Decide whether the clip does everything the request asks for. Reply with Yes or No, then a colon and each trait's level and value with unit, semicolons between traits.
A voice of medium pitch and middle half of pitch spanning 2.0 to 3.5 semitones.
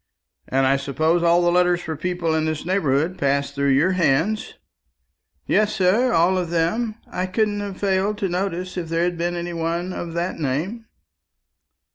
Yes: medium, 175 Hz; average, 2.9 semitones